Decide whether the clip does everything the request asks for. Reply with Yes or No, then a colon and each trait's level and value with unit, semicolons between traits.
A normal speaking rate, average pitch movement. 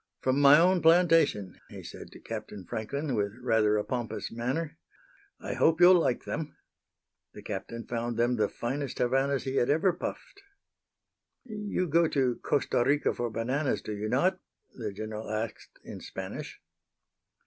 No: average, 155 wpm; wide, 6.2 semitones